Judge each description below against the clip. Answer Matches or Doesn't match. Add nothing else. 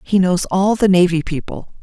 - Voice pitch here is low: Doesn't match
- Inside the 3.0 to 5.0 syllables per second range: Matches